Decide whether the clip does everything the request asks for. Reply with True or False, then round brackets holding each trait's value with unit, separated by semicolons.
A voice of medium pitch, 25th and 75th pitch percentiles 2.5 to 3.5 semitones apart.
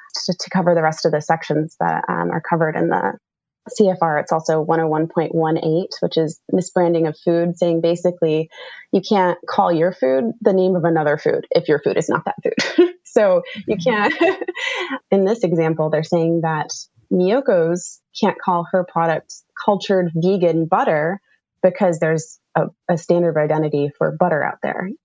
True (170 Hz; 2.9 semitones)